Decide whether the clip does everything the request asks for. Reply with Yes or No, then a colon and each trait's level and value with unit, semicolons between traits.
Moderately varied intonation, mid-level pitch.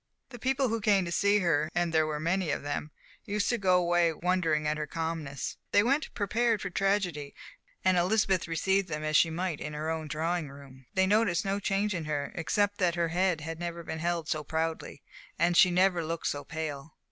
Yes: average, 3.8 semitones; medium, 170 Hz